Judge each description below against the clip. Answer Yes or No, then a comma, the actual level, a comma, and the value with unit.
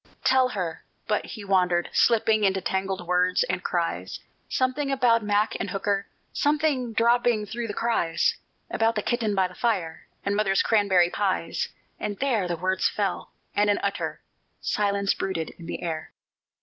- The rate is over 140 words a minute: Yes, average, 160 wpm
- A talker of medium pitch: No, high, 205 Hz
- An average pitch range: Yes, average, 3.6 semitones